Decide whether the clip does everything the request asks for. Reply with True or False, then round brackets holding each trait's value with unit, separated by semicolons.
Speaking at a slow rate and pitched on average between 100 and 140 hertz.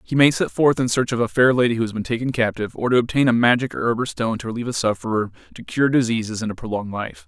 False (280 wpm; 120 Hz)